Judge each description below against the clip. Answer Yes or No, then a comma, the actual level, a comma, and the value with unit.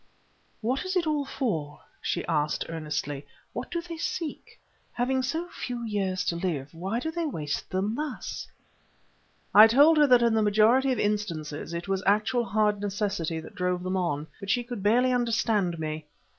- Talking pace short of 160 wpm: No, average, 175 wpm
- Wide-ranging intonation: Yes, wide, 6.7 semitones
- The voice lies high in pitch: Yes, high, 210 Hz